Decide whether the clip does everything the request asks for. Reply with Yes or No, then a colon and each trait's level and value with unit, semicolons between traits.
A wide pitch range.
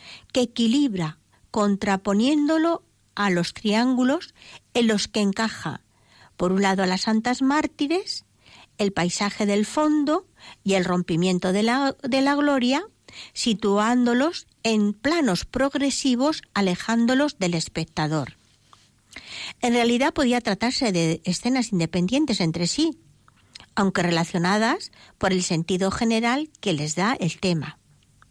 Yes: wide, 6.5 semitones